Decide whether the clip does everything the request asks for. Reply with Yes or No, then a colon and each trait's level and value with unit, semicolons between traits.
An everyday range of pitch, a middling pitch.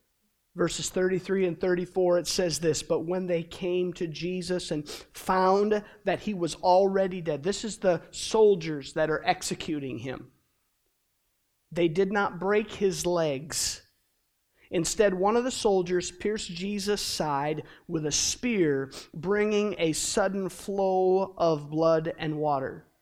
Yes: average, 3.2 semitones; medium, 180 Hz